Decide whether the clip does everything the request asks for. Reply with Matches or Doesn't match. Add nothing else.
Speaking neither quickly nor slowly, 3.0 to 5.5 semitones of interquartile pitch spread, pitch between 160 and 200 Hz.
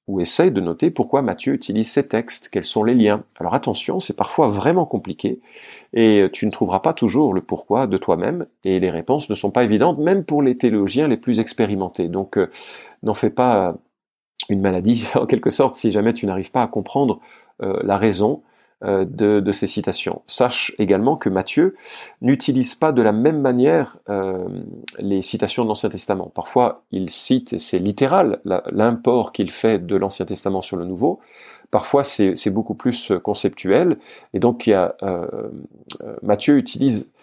Doesn't match